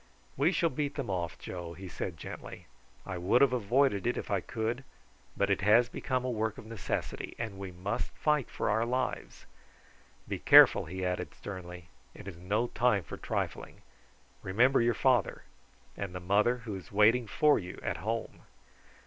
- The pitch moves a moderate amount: Yes, average, 4.8 semitones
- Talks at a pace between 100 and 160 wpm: No, average, 175 wpm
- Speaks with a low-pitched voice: Yes, low, 105 Hz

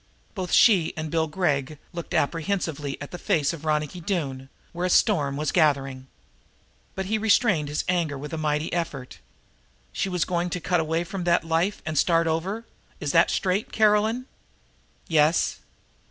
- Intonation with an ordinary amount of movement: Yes, average, 3.5 semitones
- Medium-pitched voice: Yes, medium, 165 Hz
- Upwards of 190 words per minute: No, average, 170 wpm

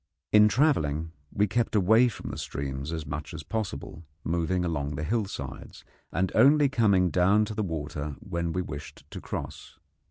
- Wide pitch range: Yes, wide, 5.9 semitones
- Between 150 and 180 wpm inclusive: Yes, average, 165 wpm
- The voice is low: Yes, very low, 90 Hz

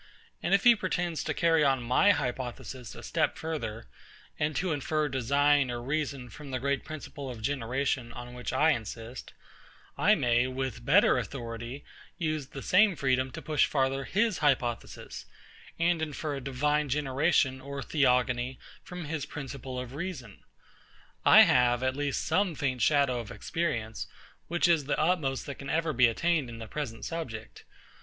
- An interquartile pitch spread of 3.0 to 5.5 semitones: Yes, average, 3.7 semitones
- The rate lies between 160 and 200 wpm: Yes, average, 165 wpm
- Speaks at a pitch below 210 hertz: Yes, low, 135 Hz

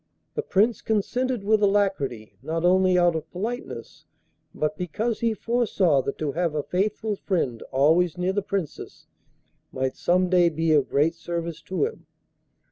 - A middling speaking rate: Yes, average, 155 wpm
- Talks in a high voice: No, medium, 180 Hz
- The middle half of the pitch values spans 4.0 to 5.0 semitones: Yes, average, 4.6 semitones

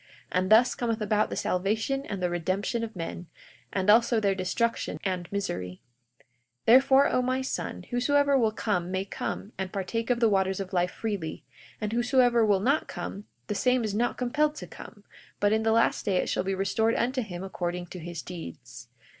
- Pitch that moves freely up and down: No, average, 4.3 semitones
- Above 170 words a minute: Yes, average, 195 wpm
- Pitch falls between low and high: No, high, 210 Hz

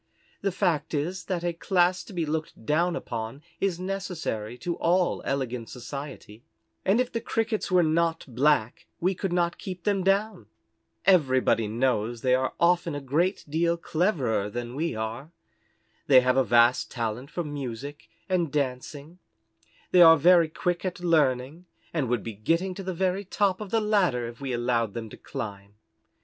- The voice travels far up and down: Yes, wide, 6.3 semitones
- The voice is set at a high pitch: No, medium, 155 Hz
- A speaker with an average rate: Yes, average, 170 wpm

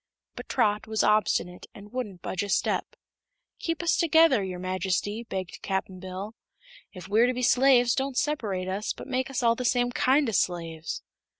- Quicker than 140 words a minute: Yes, average, 180 wpm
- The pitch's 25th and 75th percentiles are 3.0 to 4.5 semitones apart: No, average, 5.2 semitones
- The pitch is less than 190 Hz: No, high, 215 Hz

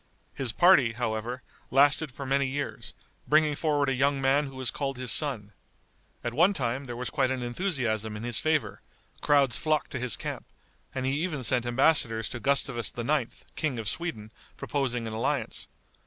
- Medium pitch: No, low, 130 Hz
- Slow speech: No, average, 175 wpm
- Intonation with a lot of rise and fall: No, average, 3.4 semitones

